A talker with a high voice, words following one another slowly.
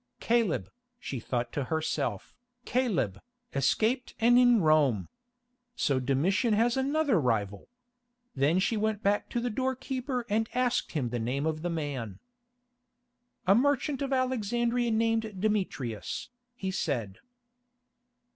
Yes: high, 205 Hz; slow, 125 wpm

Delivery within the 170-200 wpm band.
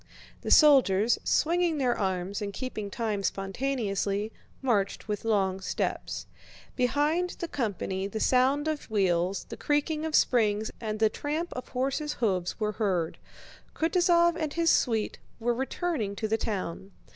No: average, 145 wpm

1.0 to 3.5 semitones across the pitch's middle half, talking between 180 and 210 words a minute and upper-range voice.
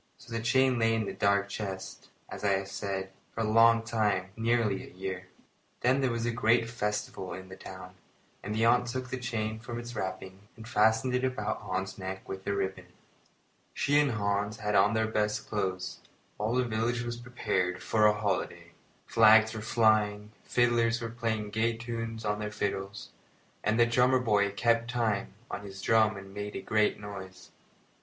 No: narrow, 2.6 semitones; average, 190 wpm; low, 110 Hz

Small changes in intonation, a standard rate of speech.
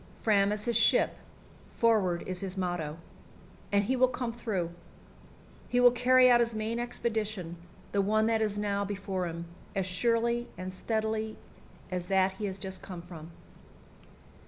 No: average, 3.7 semitones; average, 160 wpm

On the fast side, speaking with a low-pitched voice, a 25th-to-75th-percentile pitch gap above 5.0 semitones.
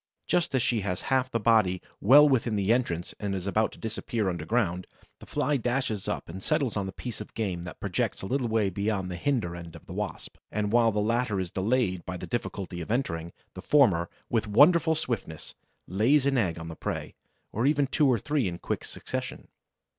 Yes: fast, 210 wpm; low, 110 Hz; wide, 5.4 semitones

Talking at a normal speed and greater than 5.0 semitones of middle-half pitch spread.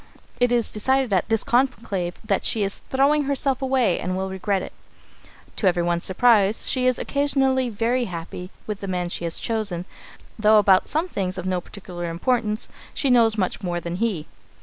Yes: average, 180 wpm; wide, 5.4 semitones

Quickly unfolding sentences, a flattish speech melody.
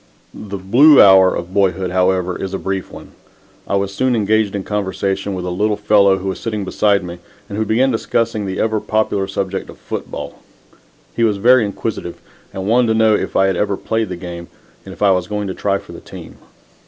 Yes: fast, 215 wpm; narrow, 2.3 semitones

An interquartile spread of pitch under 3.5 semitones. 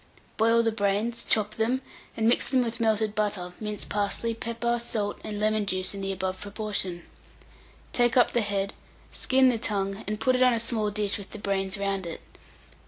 Yes: narrow, 2.6 semitones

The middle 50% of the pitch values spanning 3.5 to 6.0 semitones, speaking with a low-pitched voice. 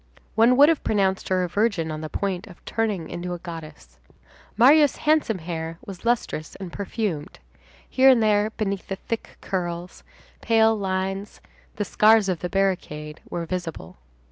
No: average, 4.3 semitones; high, 190 Hz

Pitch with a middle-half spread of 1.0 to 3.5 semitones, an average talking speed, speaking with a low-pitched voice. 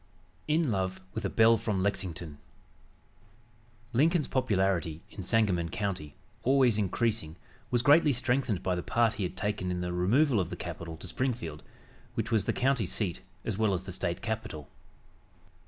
No: average, 4.9 semitones; average, 160 wpm; low, 105 Hz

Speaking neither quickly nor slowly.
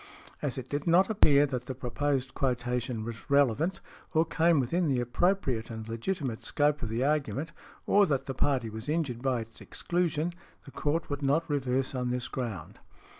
Yes: average, 175 wpm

